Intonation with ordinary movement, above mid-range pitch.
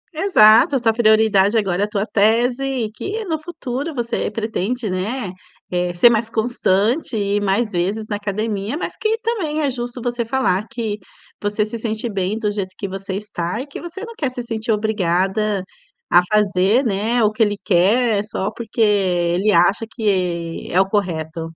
Yes: average, 3.6 semitones; high, 215 Hz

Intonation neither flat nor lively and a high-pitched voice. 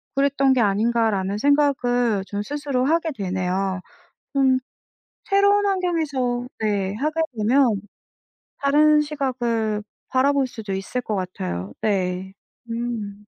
No: wide, 5.7 semitones; high, 240 Hz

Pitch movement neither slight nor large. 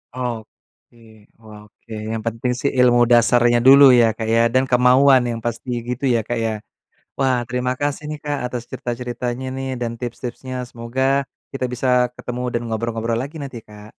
No: narrow, 1.9 semitones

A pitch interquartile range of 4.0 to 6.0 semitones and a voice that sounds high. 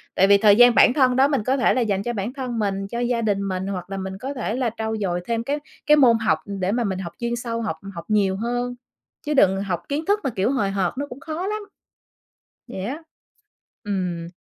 Yes: average, 4.5 semitones; high, 225 Hz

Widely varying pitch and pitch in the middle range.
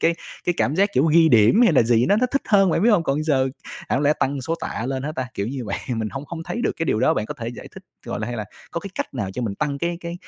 Yes: wide, 5.8 semitones; medium, 145 Hz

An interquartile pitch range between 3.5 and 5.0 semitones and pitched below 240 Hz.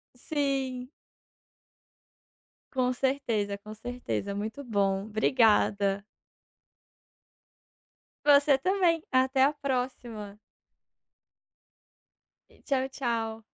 No: average, 4.2 semitones; very high, 250 Hz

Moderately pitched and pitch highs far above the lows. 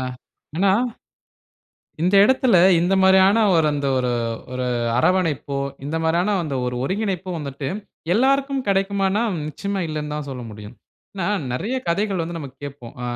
Yes: medium, 175 Hz; wide, 5.7 semitones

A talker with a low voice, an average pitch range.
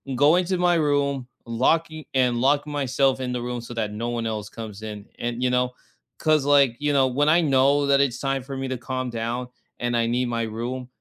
Yes: low, 130 Hz; average, 3.0 semitones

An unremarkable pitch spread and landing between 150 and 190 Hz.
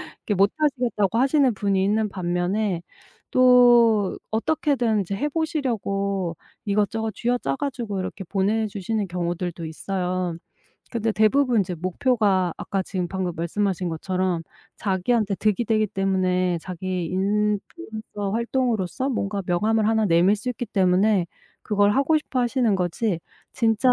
No: average, 3.7 semitones; high, 205 Hz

